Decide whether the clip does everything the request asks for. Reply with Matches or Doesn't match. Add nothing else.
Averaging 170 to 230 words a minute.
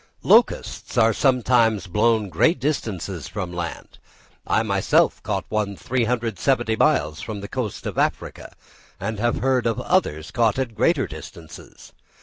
Doesn't match